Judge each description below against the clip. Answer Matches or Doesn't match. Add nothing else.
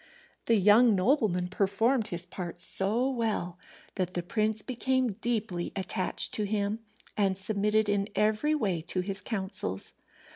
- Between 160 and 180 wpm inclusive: Doesn't match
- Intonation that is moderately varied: Matches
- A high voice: Matches